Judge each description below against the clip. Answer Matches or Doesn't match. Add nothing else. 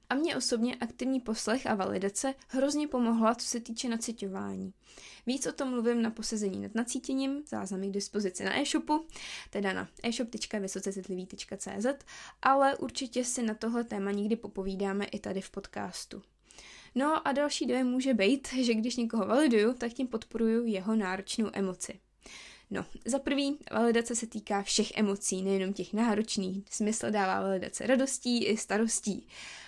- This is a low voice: Doesn't match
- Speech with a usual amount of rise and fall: Matches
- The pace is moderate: Matches